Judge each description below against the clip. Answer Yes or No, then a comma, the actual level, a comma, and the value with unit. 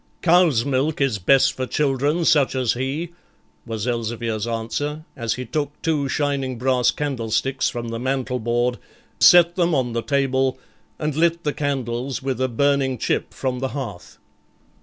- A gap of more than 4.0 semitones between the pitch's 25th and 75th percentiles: No, average, 3.3 semitones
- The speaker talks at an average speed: Yes, average, 160 wpm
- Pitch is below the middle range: Yes, low, 130 Hz